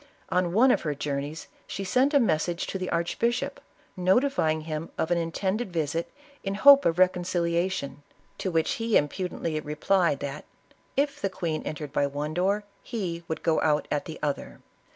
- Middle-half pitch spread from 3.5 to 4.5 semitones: Yes, average, 4.0 semitones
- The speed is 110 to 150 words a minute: No, average, 175 wpm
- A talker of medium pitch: Yes, medium, 170 Hz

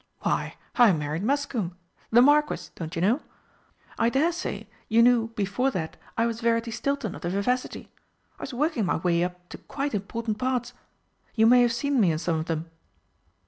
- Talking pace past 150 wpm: Yes, average, 185 wpm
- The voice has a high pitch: Yes, high, 230 Hz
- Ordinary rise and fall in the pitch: No, wide, 5.8 semitones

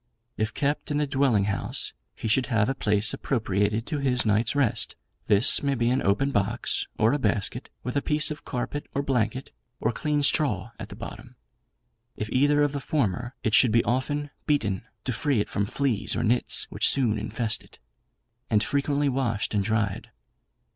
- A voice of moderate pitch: No, low, 120 Hz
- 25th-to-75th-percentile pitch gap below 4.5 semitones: No, average, 4.8 semitones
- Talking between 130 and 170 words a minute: No, average, 185 wpm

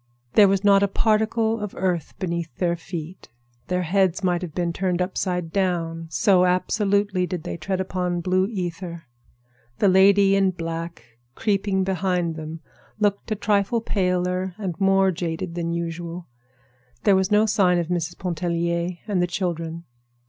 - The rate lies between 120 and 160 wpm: Yes, average, 155 wpm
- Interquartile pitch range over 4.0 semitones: No, narrow, 2.4 semitones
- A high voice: No, medium, 180 Hz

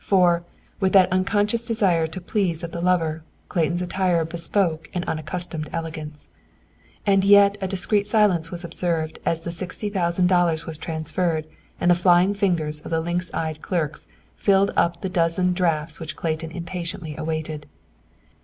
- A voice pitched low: No, medium, 175 Hz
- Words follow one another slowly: No, average, 155 wpm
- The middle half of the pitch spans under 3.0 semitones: Yes, narrow, 2.5 semitones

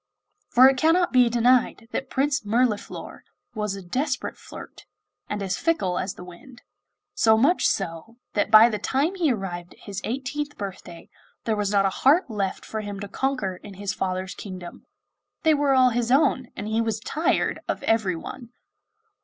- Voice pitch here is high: Yes, high, 225 Hz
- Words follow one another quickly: No, average, 175 wpm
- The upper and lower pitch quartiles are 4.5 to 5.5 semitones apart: Yes, average, 5.2 semitones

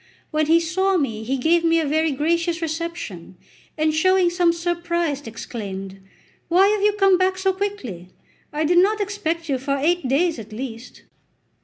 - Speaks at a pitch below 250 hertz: No, very high, 330 Hz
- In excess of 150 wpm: Yes, average, 170 wpm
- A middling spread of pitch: Yes, average, 4.7 semitones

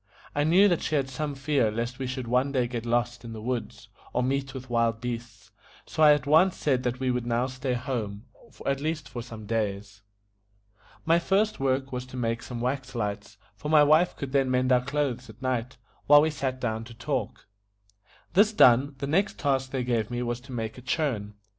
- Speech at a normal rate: No, fast, 215 wpm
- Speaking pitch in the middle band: No, low, 130 Hz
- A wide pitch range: No, average, 3.1 semitones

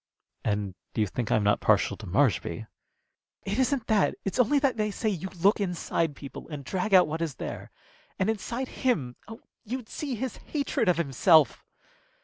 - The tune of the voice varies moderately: No, wide, 7.8 semitones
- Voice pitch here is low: No, high, 190 Hz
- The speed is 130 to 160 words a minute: No, average, 175 wpm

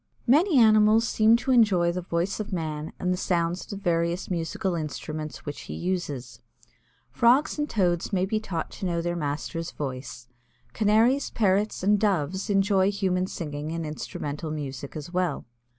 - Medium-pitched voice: Yes, medium, 180 Hz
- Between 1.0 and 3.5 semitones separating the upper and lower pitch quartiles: No, average, 4.8 semitones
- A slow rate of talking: No, average, 165 wpm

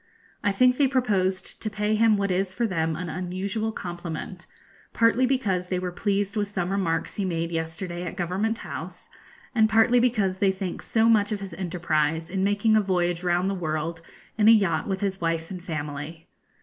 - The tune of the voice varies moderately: Yes, average, 3.5 semitones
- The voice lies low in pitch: No, high, 190 Hz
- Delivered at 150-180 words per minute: No, average, 190 wpm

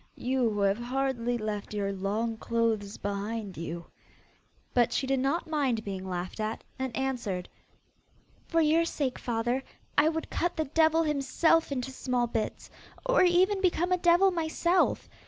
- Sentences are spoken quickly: No, average, 155 wpm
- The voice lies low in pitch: No, very high, 255 Hz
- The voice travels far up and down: Yes, wide, 6.8 semitones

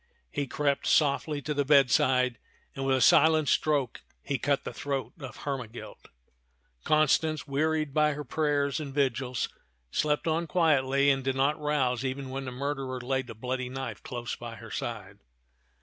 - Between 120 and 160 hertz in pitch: Yes, low, 135 Hz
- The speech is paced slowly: No, average, 165 wpm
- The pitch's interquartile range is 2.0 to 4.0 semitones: Yes, narrow, 2.5 semitones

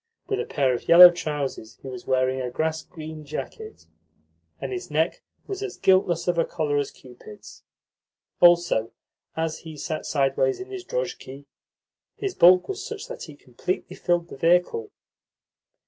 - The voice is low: No, medium, 165 Hz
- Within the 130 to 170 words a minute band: Yes, average, 160 wpm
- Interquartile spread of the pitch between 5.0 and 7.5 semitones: Yes, wide, 5.4 semitones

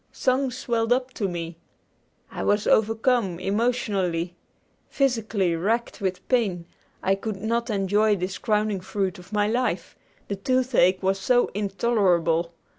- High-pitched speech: Yes, high, 205 Hz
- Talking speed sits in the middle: No, slow, 130 wpm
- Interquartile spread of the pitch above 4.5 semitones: No, average, 4.0 semitones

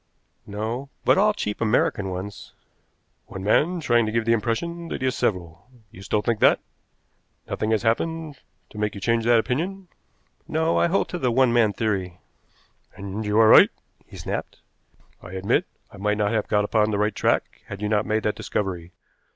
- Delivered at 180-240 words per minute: Yes, average, 190 wpm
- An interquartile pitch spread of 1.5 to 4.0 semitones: Yes, average, 3.3 semitones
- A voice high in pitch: No, low, 110 Hz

